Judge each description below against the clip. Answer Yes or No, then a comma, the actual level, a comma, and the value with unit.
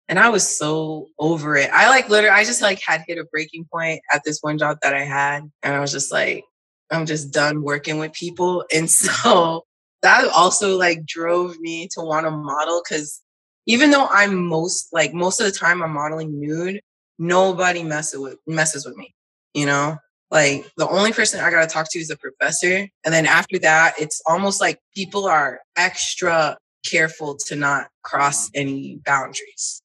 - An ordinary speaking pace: Yes, average, 190 wpm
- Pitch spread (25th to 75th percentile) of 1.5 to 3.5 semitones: Yes, average, 3.1 semitones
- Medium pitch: Yes, medium, 160 Hz